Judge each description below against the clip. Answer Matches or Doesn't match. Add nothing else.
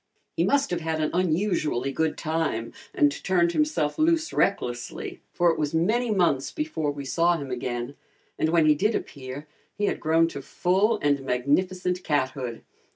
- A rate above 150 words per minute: Matches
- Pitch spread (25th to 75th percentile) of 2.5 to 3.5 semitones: Doesn't match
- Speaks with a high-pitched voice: Doesn't match